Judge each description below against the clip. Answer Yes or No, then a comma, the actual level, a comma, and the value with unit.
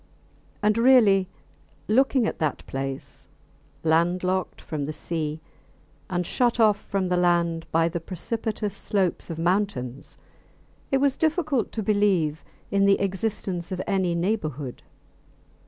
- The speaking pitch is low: No, medium, 185 Hz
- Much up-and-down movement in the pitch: No, average, 4.4 semitones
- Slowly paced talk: Yes, slow, 125 wpm